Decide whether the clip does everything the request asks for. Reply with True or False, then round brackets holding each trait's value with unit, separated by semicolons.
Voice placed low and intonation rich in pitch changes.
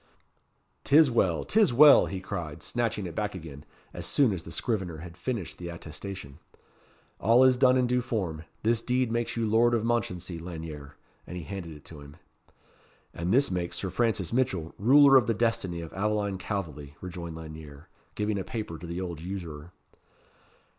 True (95 Hz; 5.9 semitones)